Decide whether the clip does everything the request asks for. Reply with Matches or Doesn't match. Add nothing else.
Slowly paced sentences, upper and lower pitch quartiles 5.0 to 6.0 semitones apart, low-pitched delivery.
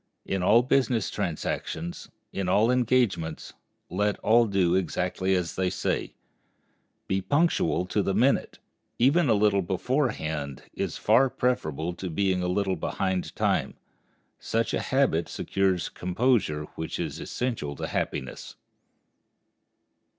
Matches